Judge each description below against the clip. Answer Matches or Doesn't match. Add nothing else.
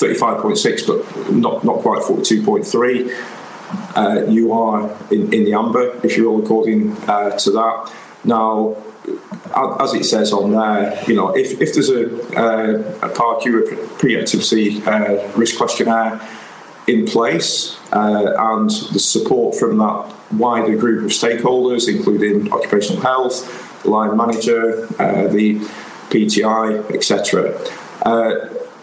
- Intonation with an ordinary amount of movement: Doesn't match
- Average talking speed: Doesn't match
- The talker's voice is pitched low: Matches